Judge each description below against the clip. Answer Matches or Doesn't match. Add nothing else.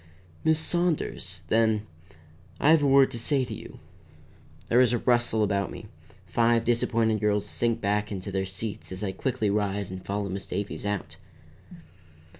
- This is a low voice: Matches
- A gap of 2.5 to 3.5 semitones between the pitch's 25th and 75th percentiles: Matches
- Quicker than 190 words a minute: Doesn't match